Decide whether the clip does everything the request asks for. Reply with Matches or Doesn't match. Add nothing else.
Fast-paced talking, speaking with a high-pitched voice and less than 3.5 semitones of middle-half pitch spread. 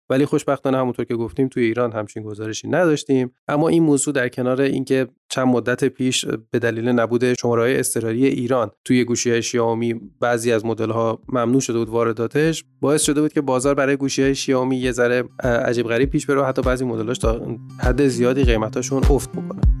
Doesn't match